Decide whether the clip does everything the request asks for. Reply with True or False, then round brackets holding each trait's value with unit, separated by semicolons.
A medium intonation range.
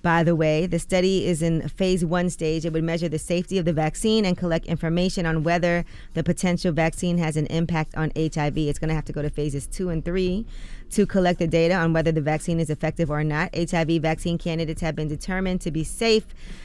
False (2.1 semitones)